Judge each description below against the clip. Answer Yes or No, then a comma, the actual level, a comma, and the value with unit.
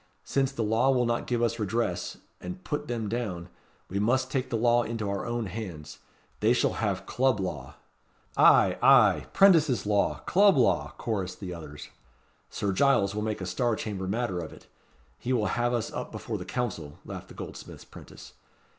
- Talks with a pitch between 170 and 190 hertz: No, low, 115 Hz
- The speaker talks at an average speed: Yes, average, 180 wpm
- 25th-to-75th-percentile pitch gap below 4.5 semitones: Yes, average, 4.1 semitones